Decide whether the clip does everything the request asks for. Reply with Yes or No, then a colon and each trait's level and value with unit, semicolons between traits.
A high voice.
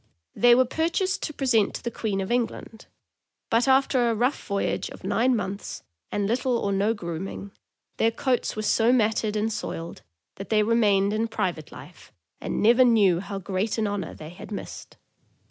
Yes: high, 220 Hz